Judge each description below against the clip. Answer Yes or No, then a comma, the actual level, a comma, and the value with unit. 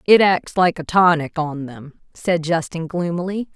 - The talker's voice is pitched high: No, medium, 170 Hz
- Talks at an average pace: Yes, average, 170 wpm